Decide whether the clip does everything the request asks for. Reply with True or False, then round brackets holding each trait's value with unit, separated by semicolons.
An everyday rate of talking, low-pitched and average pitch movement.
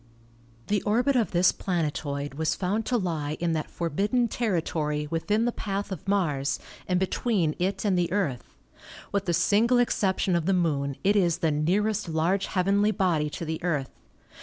False (175 wpm; 180 Hz; 4.3 semitones)